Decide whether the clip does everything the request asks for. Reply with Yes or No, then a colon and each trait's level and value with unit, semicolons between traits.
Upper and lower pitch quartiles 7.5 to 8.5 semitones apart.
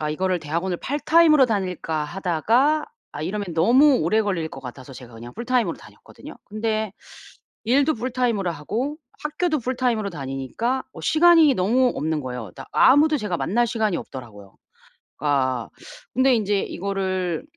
Yes: wide, 8.2 semitones